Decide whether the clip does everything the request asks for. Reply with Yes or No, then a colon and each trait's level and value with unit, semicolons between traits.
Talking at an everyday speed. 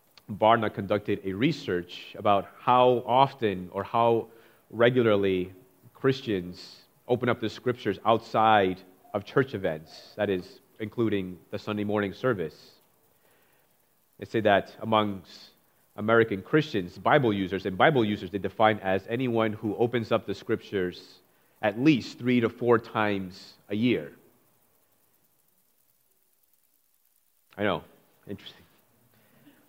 No: slow, 115 wpm